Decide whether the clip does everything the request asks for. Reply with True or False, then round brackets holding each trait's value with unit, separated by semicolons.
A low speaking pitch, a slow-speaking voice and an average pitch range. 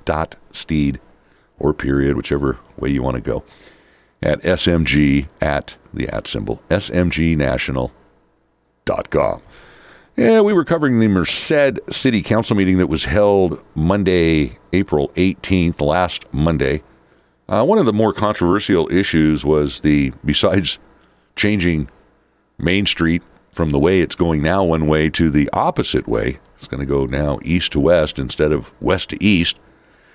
False (80 Hz; 145 wpm; 4.7 semitones)